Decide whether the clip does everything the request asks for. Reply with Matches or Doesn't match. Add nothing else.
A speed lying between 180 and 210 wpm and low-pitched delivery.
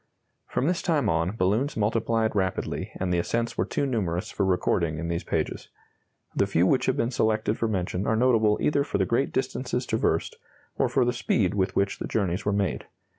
Matches